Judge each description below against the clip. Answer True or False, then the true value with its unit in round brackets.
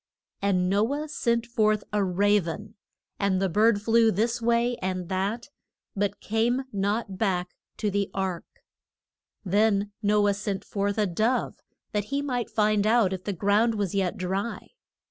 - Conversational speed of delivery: True (165 wpm)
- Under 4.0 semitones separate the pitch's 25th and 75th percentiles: True (2.7 semitones)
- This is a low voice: False (205 Hz)